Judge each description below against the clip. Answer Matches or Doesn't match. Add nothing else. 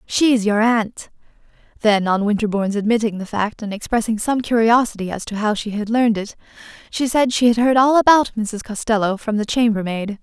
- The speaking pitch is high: Matches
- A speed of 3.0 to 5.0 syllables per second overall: Doesn't match